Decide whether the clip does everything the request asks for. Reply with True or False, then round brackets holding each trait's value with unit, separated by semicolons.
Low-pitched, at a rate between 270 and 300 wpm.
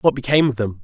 True (125 Hz; 290 wpm)